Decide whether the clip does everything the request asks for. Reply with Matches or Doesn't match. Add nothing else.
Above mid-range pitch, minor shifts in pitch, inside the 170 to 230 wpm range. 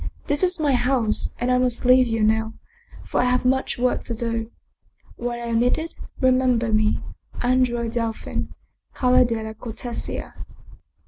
Doesn't match